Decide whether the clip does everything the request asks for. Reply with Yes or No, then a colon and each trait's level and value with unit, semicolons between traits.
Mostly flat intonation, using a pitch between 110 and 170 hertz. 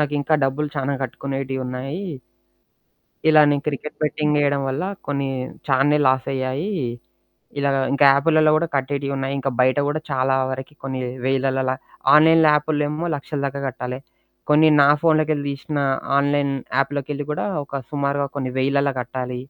Yes: narrow, 2.0 semitones; medium, 140 Hz